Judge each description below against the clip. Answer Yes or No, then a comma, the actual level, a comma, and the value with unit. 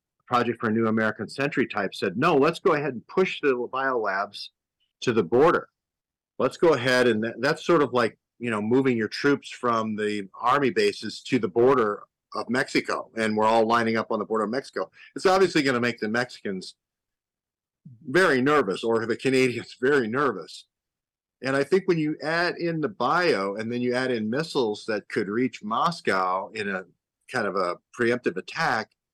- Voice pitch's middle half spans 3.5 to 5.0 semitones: Yes, average, 4.1 semitones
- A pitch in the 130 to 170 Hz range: No, low, 120 Hz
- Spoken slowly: No, average, 190 wpm